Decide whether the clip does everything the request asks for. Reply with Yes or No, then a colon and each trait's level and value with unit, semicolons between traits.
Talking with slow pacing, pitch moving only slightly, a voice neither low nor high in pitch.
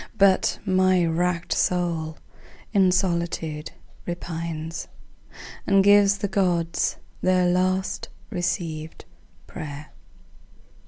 Yes: slow, 85 wpm; narrow, 2.2 semitones; medium, 175 Hz